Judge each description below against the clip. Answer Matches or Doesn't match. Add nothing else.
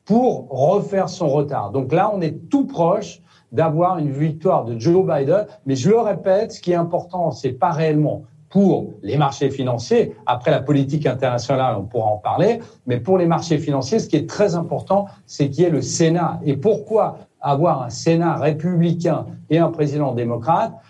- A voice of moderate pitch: Matches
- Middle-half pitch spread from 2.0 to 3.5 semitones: Doesn't match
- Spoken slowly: Doesn't match